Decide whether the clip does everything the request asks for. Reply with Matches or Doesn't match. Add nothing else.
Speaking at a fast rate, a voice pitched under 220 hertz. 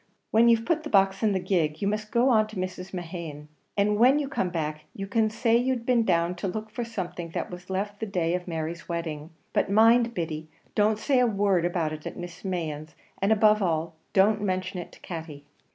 Matches